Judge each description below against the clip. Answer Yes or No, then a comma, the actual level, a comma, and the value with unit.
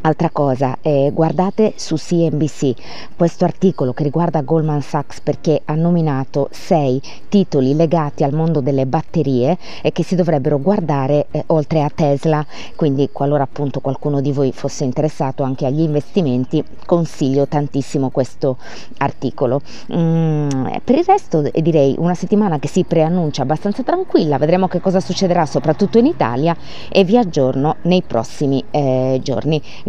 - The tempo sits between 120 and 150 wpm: Yes, average, 145 wpm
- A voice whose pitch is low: No, medium, 150 Hz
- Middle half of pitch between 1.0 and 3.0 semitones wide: No, average, 3.5 semitones